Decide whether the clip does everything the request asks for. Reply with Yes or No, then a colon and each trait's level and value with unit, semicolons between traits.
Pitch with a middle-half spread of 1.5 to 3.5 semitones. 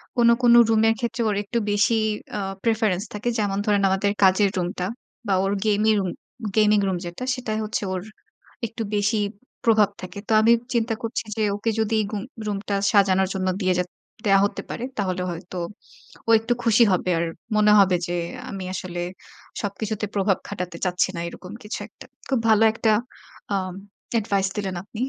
Yes: average, 2.7 semitones